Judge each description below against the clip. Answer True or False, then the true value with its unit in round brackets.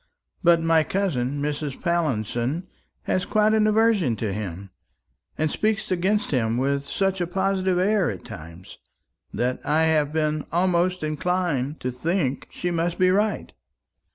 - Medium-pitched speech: True (165 Hz)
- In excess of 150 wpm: False (145 wpm)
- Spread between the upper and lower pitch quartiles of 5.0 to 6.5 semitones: True (5.6 semitones)